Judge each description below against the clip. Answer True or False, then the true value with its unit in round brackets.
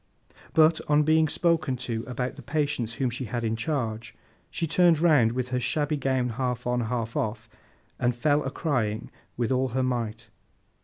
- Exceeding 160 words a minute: True (175 wpm)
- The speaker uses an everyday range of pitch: True (4.0 semitones)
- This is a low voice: True (125 Hz)